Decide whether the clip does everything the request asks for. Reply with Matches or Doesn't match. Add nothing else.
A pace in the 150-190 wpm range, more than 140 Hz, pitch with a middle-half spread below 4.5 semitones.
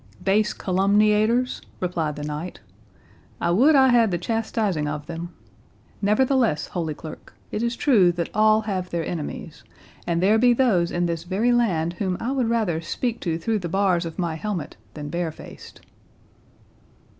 Doesn't match